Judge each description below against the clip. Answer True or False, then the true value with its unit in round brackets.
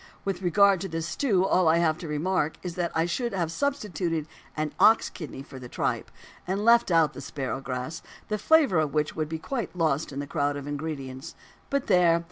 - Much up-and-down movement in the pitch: False (4.3 semitones)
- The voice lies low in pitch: False (165 Hz)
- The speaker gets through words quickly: True (210 wpm)